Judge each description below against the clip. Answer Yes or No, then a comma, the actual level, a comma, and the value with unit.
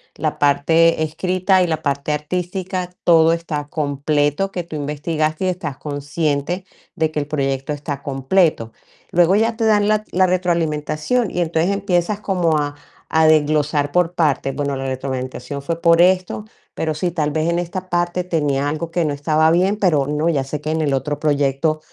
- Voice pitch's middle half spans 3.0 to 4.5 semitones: Yes, average, 3.4 semitones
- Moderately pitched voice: Yes, medium, 155 Hz